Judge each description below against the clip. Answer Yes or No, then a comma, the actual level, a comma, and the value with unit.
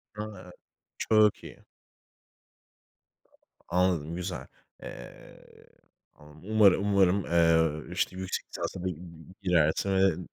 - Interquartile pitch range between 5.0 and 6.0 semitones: No, average, 2.9 semitones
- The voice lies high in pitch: No, very low, 90 Hz